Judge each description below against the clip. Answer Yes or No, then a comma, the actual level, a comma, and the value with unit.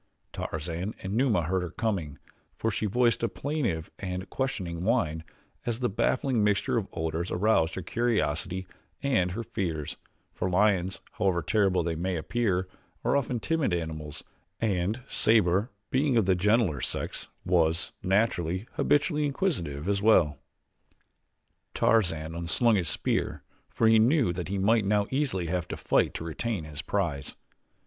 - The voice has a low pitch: Yes, very low, 95 Hz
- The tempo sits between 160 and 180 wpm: No, average, 150 wpm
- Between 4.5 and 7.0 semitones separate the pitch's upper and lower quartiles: Yes, average, 5.1 semitones